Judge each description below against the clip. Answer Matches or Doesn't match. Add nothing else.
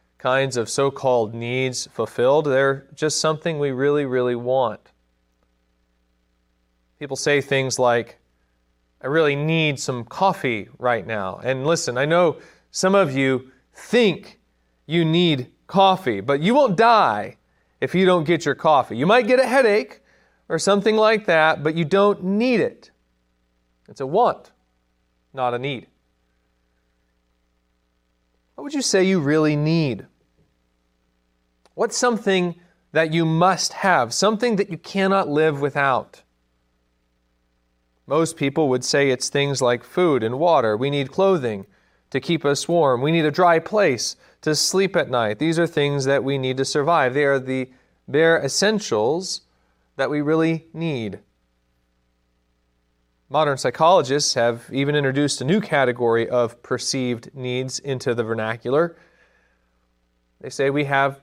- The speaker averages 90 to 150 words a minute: Matches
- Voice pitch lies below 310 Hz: Matches